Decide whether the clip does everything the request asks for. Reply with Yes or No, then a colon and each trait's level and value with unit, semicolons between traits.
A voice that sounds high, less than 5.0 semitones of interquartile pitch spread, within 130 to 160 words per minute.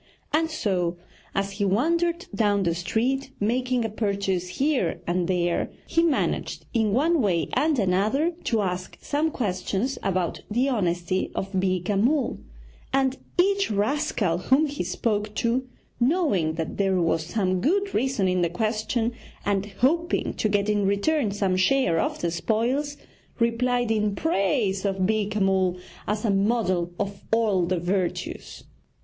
No: high, 210 Hz; wide, 5.6 semitones; average, 150 wpm